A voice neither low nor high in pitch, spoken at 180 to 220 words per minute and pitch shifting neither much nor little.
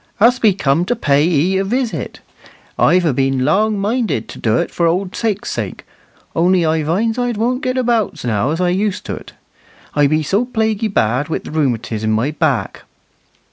No: medium, 180 Hz; average, 185 wpm; wide, 7.1 semitones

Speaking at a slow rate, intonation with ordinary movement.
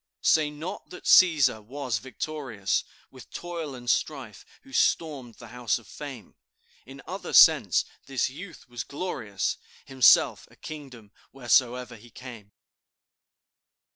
Yes: slow, 125 wpm; average, 4.1 semitones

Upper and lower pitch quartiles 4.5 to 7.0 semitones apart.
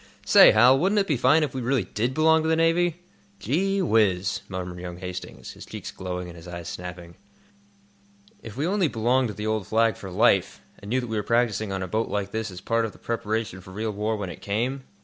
Yes: wide, 5.6 semitones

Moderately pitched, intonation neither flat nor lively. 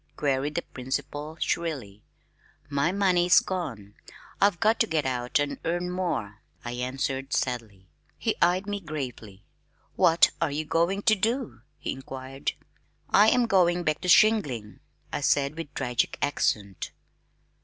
No: medium, 150 Hz; wide, 5.7 semitones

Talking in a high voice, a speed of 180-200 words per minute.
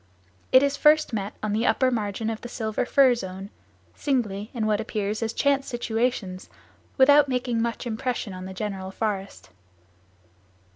No: high, 225 Hz; average, 155 wpm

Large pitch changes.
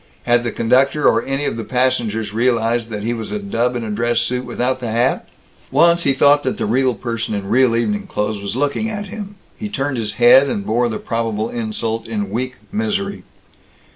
No: average, 3.3 semitones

